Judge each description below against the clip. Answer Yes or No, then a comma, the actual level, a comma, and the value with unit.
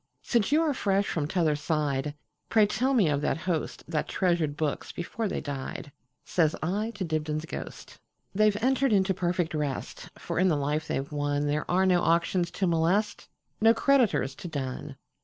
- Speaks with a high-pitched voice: No, medium, 170 Hz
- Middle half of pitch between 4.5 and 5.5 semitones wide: Yes, average, 5.2 semitones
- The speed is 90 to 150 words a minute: No, average, 160 wpm